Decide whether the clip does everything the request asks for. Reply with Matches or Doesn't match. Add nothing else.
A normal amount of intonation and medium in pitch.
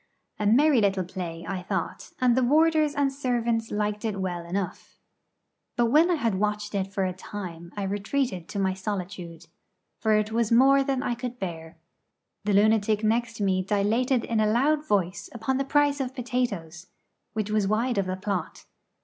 Doesn't match